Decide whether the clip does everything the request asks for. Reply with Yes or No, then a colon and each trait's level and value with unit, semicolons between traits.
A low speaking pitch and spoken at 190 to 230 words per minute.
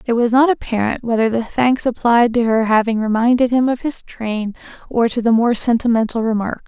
No: high, 235 Hz; average, 200 wpm